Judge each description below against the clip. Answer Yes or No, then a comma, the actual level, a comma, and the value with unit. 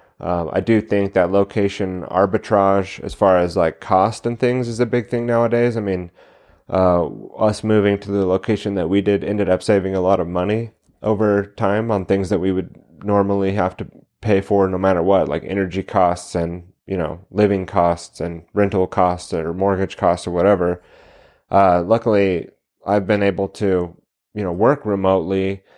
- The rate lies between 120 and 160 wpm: No, average, 180 wpm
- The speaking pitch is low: Yes, low, 100 Hz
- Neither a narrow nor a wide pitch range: No, narrow, 2.1 semitones